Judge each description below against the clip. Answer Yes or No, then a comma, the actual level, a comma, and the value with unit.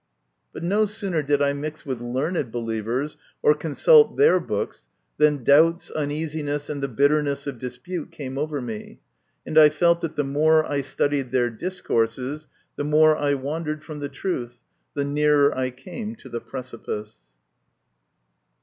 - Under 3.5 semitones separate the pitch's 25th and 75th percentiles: Yes, average, 3.1 semitones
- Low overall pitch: No, medium, 145 Hz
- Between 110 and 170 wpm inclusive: Yes, average, 155 wpm